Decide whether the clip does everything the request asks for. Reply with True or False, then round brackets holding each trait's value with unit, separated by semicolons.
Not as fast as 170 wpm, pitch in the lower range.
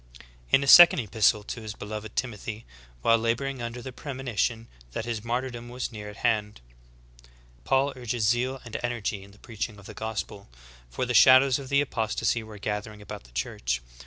False (180 wpm; 115 Hz)